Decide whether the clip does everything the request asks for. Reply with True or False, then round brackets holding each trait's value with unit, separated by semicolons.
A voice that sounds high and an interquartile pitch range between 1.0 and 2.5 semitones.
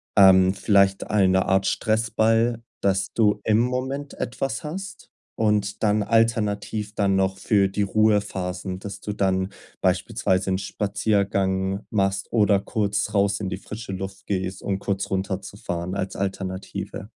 False (100 Hz; 2.0 semitones)